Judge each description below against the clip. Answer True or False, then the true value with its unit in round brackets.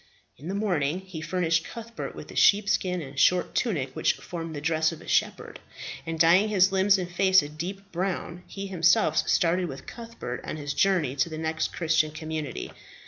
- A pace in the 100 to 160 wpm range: False (190 wpm)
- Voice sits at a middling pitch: True (170 Hz)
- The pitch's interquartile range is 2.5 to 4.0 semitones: True (3.4 semitones)